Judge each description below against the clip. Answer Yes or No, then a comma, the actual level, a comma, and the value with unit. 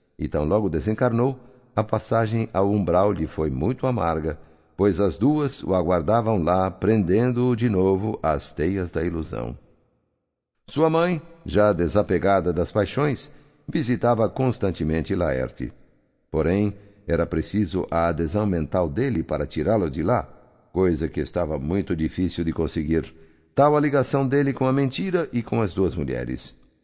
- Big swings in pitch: Yes, wide, 5.8 semitones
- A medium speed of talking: Yes, average, 145 wpm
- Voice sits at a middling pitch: No, very low, 95 Hz